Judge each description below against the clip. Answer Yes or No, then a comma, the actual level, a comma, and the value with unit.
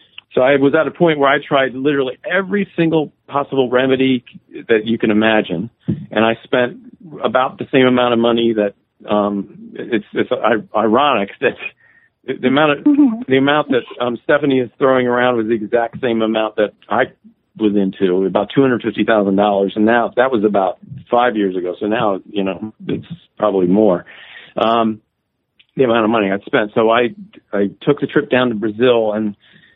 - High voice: No, low, 120 Hz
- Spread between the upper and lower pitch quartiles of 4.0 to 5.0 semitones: Yes, average, 4.4 semitones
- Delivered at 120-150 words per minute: No, average, 185 wpm